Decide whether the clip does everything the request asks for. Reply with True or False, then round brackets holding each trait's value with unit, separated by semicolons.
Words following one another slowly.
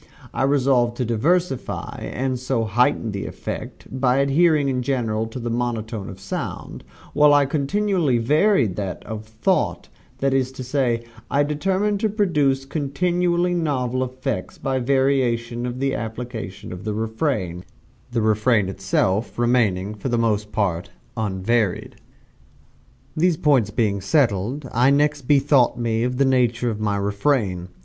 False (145 wpm)